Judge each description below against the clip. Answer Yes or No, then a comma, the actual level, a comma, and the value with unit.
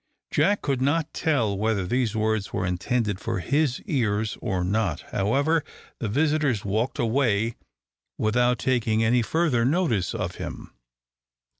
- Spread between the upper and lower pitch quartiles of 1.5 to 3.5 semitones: No, average, 5.0 semitones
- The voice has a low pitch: Yes, low, 115 Hz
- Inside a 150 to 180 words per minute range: No, slow, 135 wpm